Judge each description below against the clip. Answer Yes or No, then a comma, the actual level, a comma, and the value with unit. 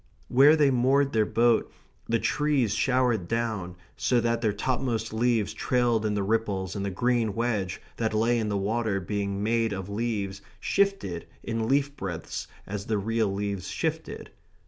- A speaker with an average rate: Yes, average, 165 wpm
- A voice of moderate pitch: No, low, 115 Hz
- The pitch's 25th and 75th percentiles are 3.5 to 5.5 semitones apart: No, average, 3.1 semitones